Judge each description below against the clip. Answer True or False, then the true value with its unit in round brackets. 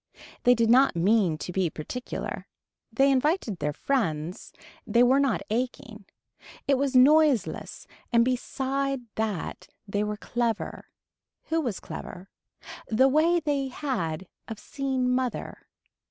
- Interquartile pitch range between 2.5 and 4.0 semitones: False (4.6 semitones)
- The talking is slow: True (125 wpm)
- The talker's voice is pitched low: False (250 Hz)